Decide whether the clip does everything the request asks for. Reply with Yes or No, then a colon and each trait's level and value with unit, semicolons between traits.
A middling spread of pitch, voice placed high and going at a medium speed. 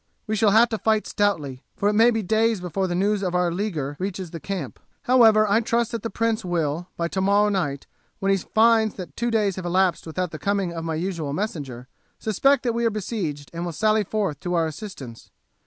No: average, 4.4 semitones; high, 195 Hz; fast, 220 wpm